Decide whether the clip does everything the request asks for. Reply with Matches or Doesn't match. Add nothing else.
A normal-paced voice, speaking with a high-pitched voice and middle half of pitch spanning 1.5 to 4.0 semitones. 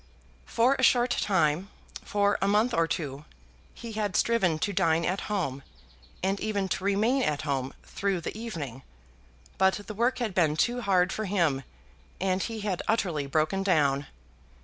Doesn't match